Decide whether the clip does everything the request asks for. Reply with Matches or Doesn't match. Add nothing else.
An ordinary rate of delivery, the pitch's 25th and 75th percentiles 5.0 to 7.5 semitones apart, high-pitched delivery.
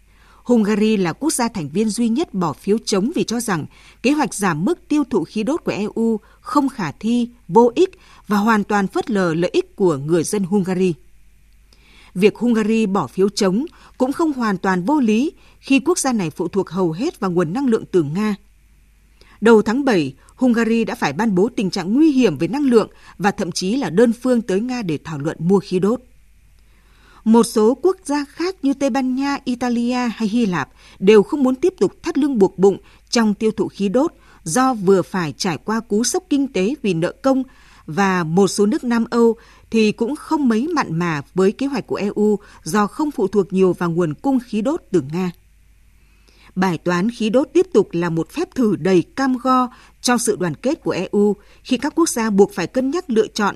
Matches